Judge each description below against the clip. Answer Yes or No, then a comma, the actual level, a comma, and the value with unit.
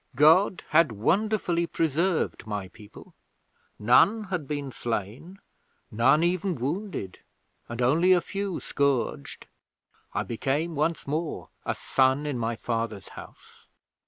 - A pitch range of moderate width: No, wide, 6.5 semitones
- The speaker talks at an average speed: No, slow, 120 wpm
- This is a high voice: No, medium, 145 Hz